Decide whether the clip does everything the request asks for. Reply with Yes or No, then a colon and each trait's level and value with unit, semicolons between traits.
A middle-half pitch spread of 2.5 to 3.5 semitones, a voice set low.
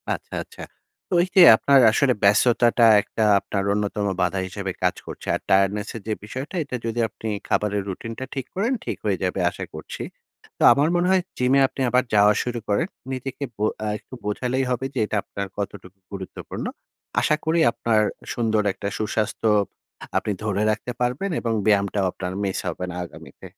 No: average, 4.2 semitones; low, 110 Hz